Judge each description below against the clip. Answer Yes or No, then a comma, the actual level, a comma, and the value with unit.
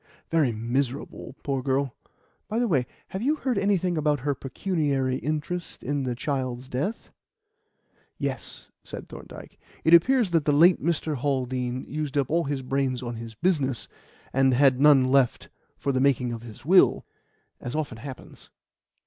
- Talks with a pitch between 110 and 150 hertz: Yes, medium, 140 Hz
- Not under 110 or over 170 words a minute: Yes, average, 155 wpm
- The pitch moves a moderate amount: Yes, average, 3.8 semitones